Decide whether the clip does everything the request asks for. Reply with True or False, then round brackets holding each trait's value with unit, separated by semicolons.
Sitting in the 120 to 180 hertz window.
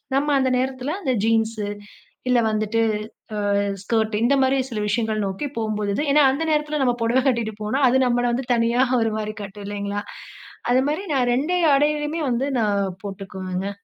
False (235 Hz)